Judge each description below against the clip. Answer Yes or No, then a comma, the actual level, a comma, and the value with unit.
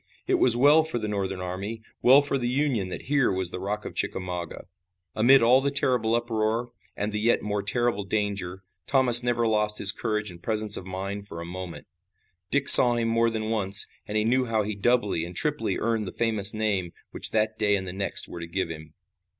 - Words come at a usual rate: No, fast, 215 wpm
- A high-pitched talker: No, low, 105 Hz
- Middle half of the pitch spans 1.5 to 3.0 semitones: No, average, 3.5 semitones